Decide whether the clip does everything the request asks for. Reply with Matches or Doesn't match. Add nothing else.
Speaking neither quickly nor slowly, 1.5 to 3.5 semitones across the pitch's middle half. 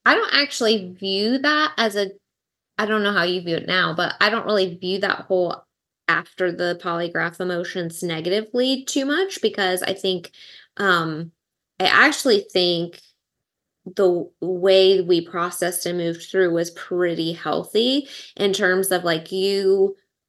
Matches